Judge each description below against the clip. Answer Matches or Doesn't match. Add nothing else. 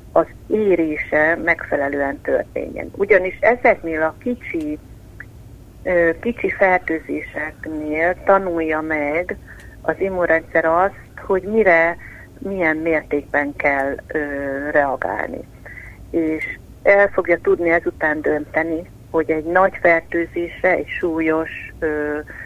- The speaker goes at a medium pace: Doesn't match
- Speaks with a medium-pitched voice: Matches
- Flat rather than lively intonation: Doesn't match